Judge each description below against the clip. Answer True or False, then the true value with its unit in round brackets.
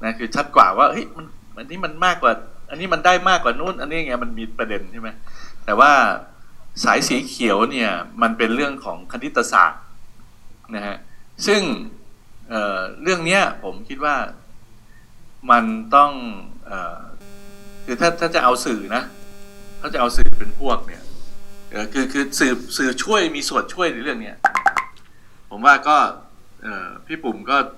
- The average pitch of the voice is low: True (120 Hz)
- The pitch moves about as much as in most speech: False (8.8 semitones)